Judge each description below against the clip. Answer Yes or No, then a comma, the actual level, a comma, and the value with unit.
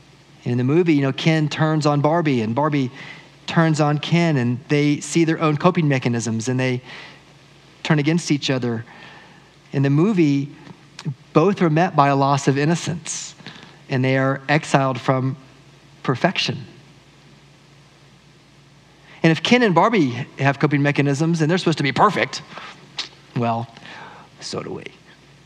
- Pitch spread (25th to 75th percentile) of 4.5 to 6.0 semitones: No, average, 2.7 semitones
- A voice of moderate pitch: Yes, medium, 150 Hz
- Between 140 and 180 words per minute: Yes, average, 145 wpm